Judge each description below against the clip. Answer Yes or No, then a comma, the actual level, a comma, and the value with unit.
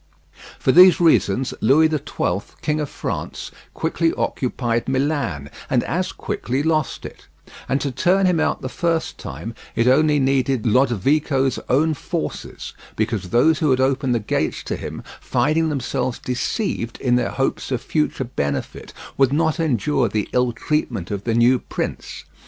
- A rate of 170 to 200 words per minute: No, average, 160 wpm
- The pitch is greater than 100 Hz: Yes, low, 135 Hz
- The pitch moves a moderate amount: Yes, average, 4.5 semitones